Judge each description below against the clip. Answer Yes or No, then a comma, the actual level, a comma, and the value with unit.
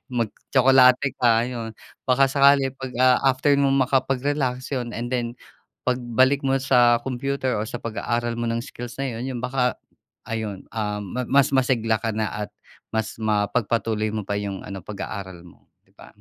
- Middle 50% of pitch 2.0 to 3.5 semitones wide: Yes, average, 2.8 semitones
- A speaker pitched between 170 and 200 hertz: No, low, 120 Hz